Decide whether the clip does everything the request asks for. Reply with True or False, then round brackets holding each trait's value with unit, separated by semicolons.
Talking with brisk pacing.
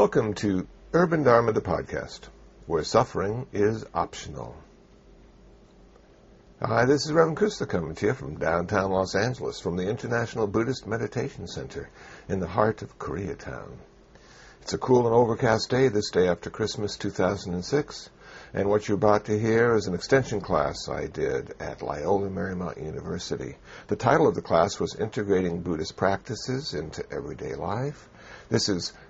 False (155 wpm)